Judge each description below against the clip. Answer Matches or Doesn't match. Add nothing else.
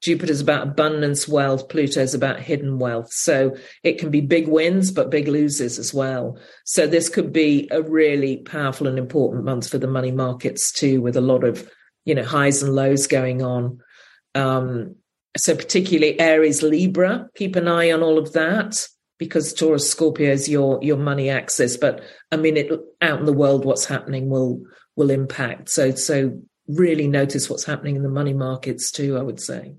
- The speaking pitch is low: Doesn't match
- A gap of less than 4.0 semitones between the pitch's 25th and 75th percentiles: Matches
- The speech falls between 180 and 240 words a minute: Matches